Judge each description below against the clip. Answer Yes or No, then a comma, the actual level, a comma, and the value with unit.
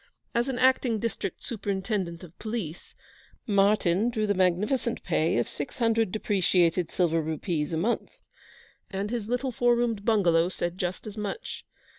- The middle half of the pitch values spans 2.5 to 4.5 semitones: No, average, 4.9 semitones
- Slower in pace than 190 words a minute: Yes, average, 150 wpm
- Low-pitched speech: No, high, 200 Hz